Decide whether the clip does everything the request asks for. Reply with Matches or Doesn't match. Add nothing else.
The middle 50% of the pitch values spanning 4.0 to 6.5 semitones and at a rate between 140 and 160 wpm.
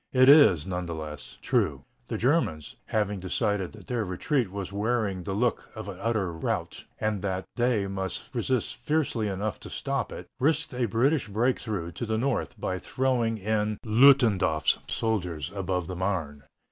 Doesn't match